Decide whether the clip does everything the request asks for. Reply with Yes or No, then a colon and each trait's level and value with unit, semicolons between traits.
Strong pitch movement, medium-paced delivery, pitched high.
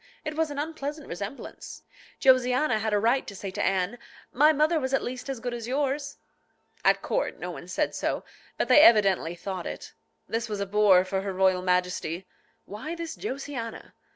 Yes: wide, 6.6 semitones; average, 185 wpm; high, 235 Hz